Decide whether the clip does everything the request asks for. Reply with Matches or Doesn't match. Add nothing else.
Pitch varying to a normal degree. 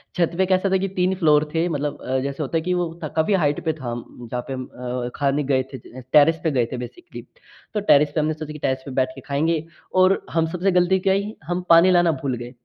Matches